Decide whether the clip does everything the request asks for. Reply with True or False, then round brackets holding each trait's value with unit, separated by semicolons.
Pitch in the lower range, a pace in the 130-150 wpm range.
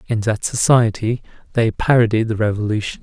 True (110 Hz; 140 wpm)